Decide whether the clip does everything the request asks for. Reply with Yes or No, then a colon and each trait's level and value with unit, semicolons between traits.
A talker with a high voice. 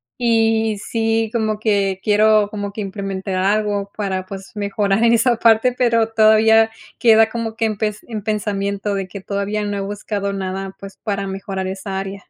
Yes: high, 205 Hz